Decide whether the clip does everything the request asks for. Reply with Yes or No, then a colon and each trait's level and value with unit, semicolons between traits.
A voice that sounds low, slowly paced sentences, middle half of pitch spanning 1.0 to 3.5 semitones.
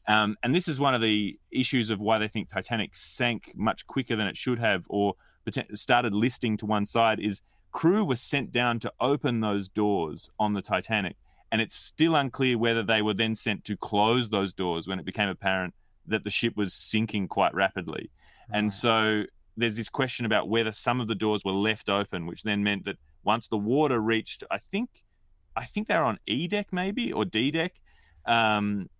No: low, 110 Hz; average, 200 wpm; average, 2.8 semitones